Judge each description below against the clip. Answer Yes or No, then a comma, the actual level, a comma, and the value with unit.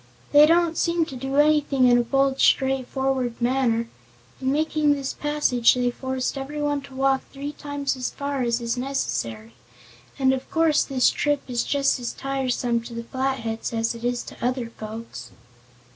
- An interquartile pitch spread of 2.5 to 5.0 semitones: Yes, average, 2.8 semitones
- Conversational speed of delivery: Yes, average, 170 wpm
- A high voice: Yes, very high, 265 Hz